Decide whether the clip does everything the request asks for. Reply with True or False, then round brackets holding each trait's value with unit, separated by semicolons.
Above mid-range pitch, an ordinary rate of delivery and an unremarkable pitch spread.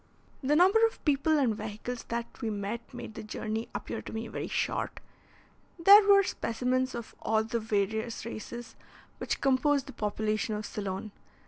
True (230 Hz; 160 wpm; 4.0 semitones)